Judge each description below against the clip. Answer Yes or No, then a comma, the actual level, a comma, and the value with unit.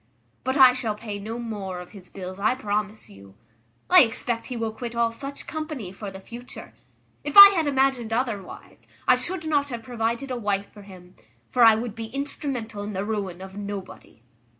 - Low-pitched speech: No, high, 225 Hz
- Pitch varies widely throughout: No, average, 4.0 semitones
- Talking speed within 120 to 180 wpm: No, average, 195 wpm